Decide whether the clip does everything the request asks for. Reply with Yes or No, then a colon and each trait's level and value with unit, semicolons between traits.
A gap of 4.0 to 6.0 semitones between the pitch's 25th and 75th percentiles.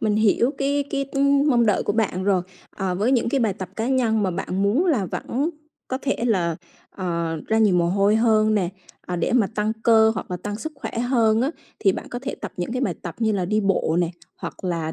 Yes: average, 4.6 semitones